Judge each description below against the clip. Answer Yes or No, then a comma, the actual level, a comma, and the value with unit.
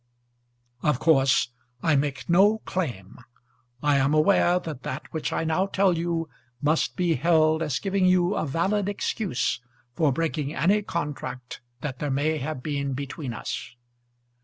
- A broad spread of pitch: No, average, 4.0 semitones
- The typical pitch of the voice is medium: Yes, medium, 155 Hz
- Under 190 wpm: Yes, average, 150 wpm